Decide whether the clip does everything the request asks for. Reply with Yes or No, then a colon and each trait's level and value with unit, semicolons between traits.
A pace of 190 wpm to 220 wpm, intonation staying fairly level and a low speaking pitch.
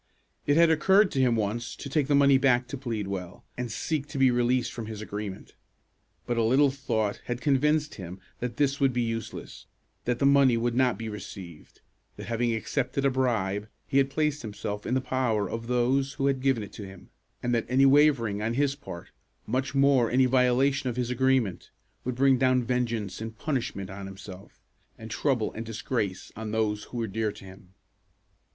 No: average, 195 wpm; average, 3.7 semitones; low, 120 Hz